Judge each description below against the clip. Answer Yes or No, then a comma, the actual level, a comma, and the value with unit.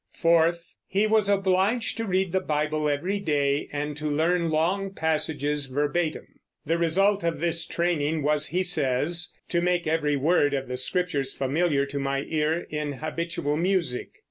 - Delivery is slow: No, average, 160 wpm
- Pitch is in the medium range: Yes, medium, 160 Hz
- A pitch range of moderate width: Yes, average, 3.4 semitones